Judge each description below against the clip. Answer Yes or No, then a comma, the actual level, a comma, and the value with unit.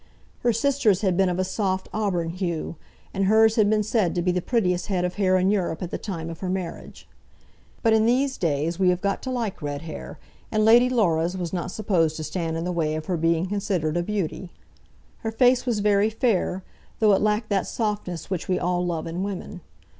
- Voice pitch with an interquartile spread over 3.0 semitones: Yes, average, 3.7 semitones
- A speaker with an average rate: No, fast, 220 wpm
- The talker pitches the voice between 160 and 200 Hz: Yes, medium, 185 Hz